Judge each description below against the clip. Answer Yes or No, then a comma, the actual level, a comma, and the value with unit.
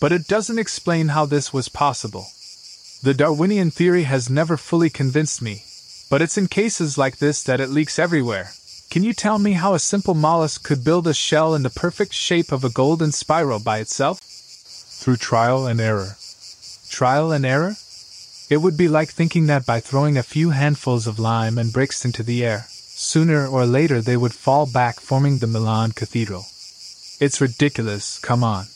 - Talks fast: Yes, fast, 185 wpm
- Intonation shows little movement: No, average, 5.2 semitones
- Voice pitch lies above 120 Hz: Yes, medium, 140 Hz